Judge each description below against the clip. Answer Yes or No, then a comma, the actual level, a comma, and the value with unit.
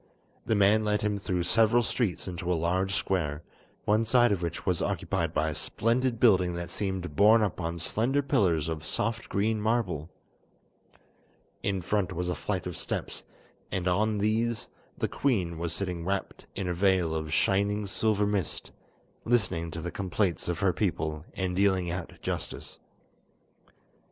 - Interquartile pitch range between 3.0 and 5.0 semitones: Yes, average, 3.7 semitones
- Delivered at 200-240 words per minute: No, average, 160 wpm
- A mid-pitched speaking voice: No, very low, 95 Hz